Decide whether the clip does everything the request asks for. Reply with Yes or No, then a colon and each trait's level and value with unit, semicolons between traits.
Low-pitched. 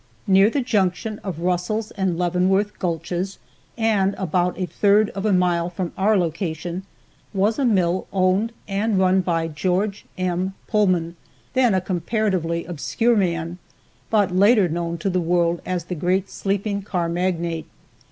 No: medium, 185 Hz